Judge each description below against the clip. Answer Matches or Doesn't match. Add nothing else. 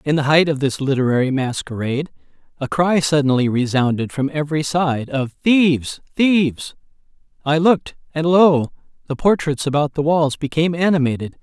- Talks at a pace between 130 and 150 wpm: Matches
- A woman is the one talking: Doesn't match